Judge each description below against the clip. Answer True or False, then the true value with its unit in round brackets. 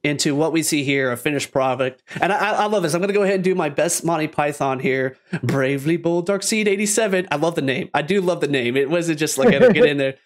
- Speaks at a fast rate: True (275 wpm)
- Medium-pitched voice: True (160 Hz)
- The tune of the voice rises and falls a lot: True (6.0 semitones)